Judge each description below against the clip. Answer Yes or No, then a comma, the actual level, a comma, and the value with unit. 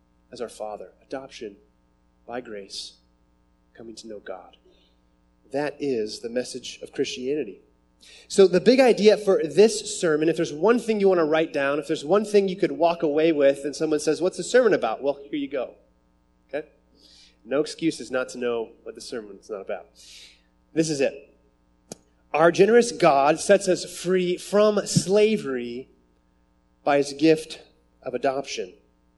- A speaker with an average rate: Yes, average, 165 wpm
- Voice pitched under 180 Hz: Yes, medium, 140 Hz